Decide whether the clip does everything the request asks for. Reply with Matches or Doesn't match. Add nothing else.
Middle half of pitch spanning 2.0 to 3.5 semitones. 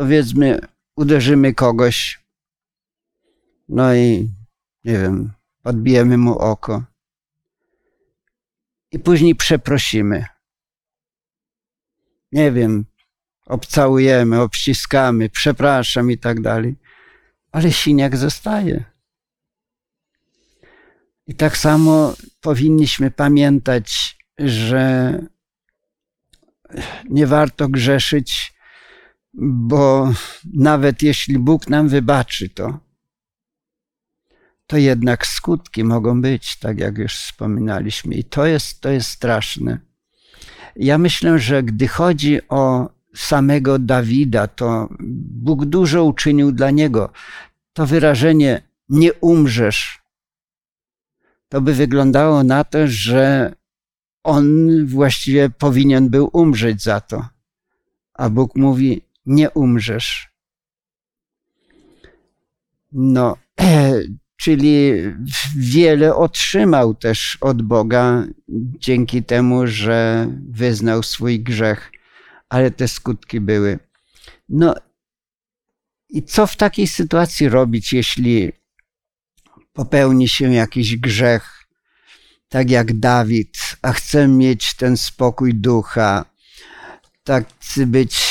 Doesn't match